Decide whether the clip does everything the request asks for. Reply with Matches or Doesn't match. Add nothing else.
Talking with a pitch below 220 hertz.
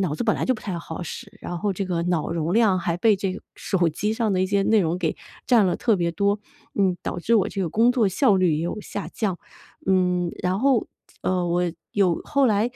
Matches